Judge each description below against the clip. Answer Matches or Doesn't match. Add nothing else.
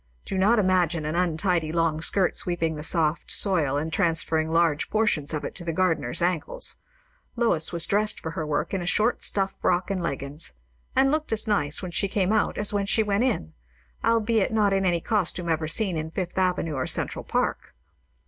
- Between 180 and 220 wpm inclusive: Matches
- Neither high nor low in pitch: Matches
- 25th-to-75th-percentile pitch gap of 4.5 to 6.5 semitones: Doesn't match